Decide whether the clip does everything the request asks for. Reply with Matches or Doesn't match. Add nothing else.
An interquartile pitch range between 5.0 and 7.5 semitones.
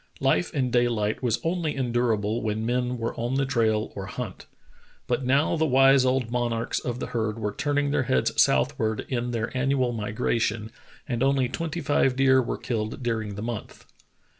Doesn't match